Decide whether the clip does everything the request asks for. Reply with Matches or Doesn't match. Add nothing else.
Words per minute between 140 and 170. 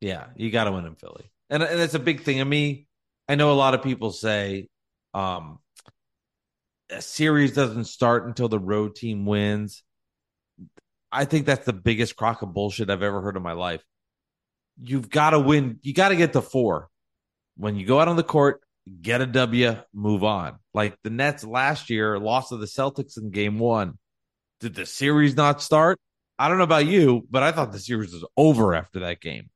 Doesn't match